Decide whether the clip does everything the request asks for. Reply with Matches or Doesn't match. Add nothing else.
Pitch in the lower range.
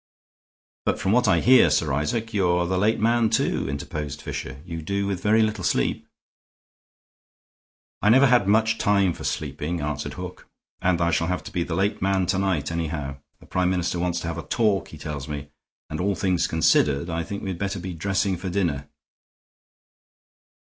Matches